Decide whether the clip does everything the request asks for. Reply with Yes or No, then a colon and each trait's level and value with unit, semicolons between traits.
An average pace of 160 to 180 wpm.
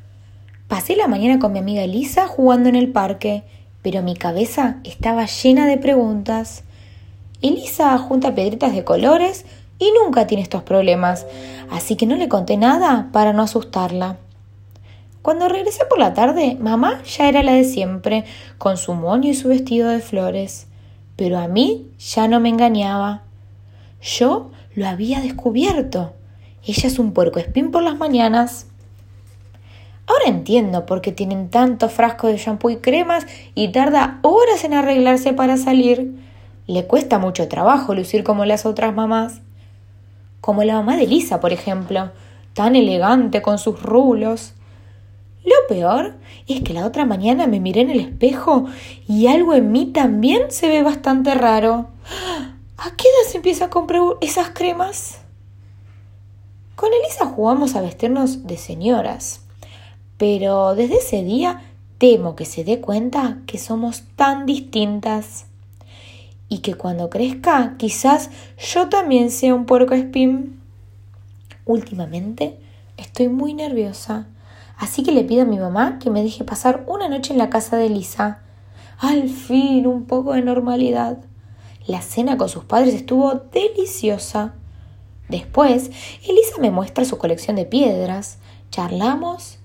No: average, 145 wpm